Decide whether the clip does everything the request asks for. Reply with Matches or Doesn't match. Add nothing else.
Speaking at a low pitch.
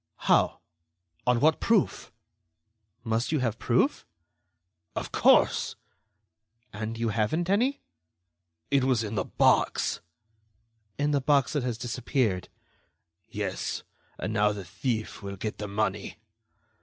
Matches